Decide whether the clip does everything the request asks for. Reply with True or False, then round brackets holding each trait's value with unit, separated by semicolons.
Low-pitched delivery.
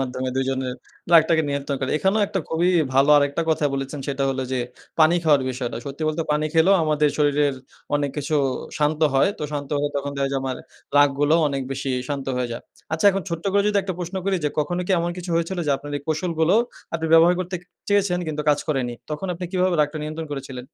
False (150 Hz)